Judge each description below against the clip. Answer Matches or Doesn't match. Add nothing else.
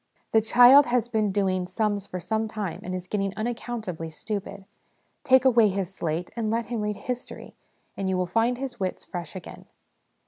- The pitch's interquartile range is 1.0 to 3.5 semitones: Doesn't match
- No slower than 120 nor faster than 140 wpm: Doesn't match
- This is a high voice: Matches